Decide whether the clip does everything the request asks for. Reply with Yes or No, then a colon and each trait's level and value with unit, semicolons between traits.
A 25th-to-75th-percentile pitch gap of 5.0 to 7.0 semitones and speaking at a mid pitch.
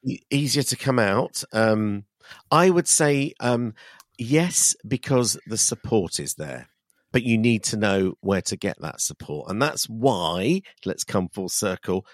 No: wide, 5.6 semitones; low, 120 Hz